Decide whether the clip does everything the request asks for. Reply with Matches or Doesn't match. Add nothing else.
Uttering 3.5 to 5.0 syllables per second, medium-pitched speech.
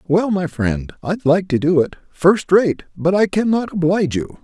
Matches